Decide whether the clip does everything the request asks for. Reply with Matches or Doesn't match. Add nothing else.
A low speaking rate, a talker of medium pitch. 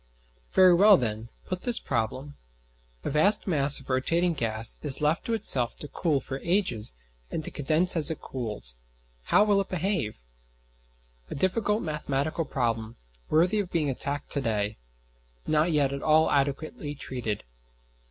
Doesn't match